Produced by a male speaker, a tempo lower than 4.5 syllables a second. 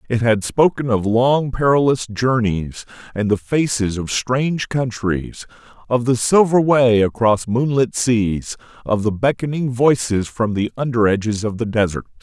Yes: male; 4.3 syllables/s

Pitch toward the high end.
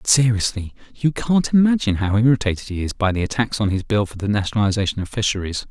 No: low, 110 Hz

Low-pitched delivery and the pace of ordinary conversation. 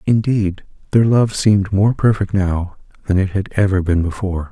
Yes: low, 100 Hz; average, 175 wpm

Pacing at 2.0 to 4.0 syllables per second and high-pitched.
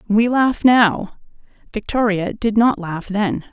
Yes: 3.6 syllables/s; high, 210 Hz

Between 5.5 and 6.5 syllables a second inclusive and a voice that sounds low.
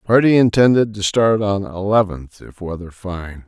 No: 4.5 syllables/s; low, 100 Hz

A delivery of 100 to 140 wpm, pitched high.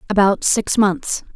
Yes: slow, 135 wpm; high, 210 Hz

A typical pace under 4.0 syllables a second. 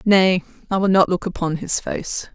No: 4.6 syllables/s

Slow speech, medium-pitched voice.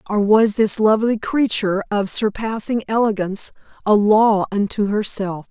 No: slow, 130 wpm; high, 210 Hz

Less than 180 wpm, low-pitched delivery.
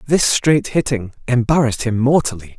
Yes: average, 140 wpm; low, 125 Hz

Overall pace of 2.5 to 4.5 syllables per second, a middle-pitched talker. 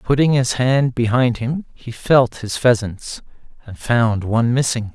No: 4.1 syllables/s; low, 120 Hz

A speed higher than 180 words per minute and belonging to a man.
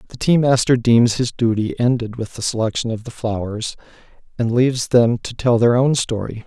Yes: average, 195 wpm; male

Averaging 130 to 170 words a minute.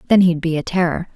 No: fast, 260 wpm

